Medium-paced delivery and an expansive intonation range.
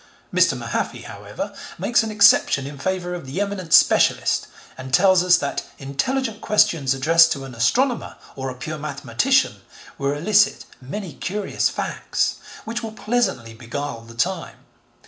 Yes: average, 145 wpm; wide, 7.5 semitones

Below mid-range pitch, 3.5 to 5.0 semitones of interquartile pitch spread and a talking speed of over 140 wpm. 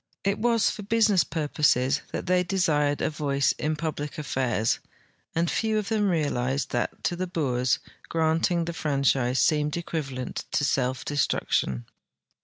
No: medium, 150 Hz; average, 4.3 semitones; average, 150 wpm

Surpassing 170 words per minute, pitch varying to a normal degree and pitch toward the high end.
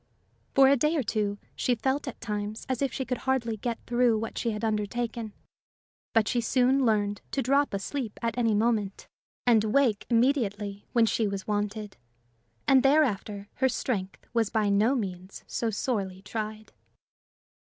No: average, 165 wpm; average, 3.4 semitones; high, 225 Hz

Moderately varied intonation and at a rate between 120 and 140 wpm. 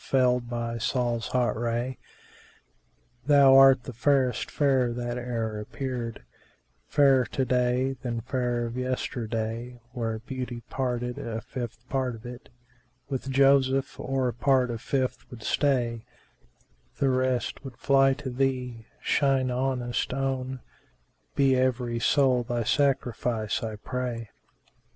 No: narrow, 2.0 semitones; slow, 135 wpm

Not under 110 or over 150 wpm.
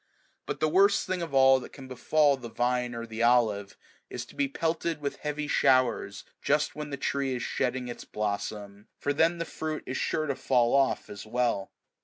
No: average, 200 wpm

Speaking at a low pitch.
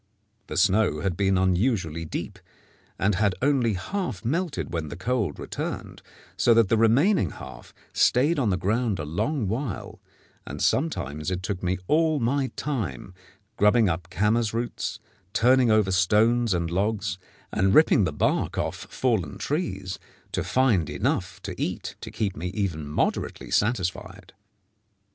Yes: low, 105 Hz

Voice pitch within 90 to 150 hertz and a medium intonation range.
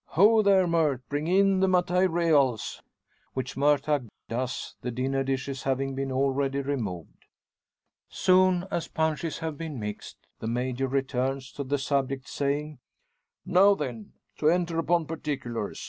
Yes: medium, 140 Hz; average, 4.1 semitones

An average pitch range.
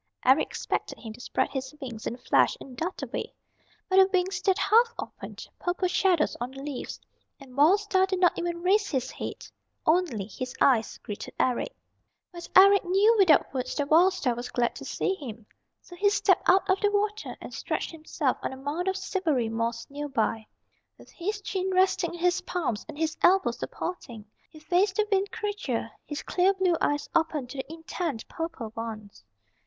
No: wide, 6.6 semitones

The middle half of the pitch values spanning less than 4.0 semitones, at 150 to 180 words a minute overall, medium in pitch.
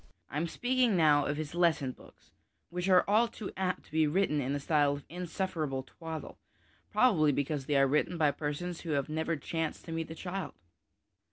No: average, 3.5 semitones; average, 195 wpm; medium, 160 Hz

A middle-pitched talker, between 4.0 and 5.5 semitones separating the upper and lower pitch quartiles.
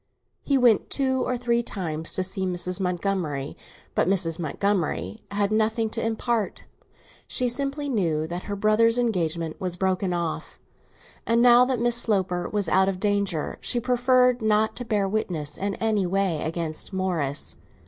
No: high, 200 Hz; average, 4.7 semitones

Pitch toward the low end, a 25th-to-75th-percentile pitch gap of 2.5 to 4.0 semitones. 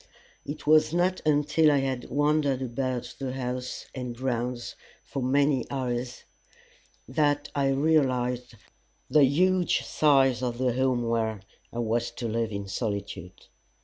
Yes: low, 130 Hz; average, 3.3 semitones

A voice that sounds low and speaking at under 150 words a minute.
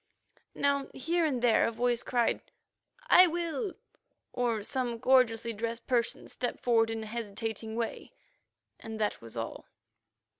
No: high, 235 Hz; average, 140 wpm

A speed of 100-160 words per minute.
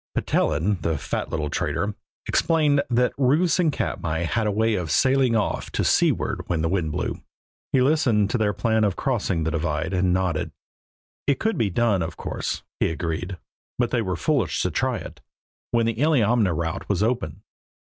No: average, 180 wpm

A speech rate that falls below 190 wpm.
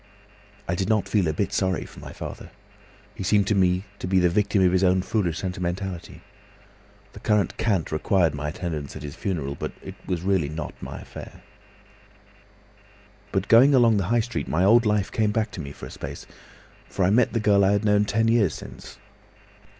No: average, 200 wpm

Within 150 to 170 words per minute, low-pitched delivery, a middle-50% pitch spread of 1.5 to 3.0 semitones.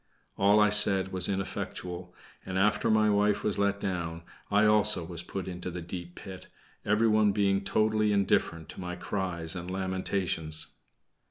Yes: average, 155 wpm; very low, 95 Hz; average, 2.7 semitones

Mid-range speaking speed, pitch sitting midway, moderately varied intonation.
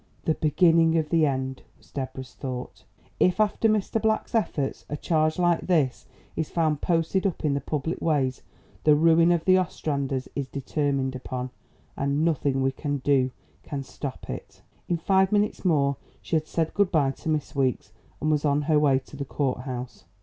Yes: average, 180 wpm; medium, 150 Hz; average, 3.6 semitones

